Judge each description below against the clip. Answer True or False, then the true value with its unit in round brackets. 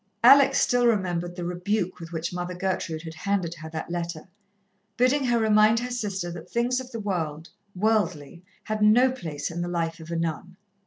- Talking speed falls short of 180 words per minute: False (190 wpm)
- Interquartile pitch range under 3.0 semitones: False (4.6 semitones)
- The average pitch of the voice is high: False (180 Hz)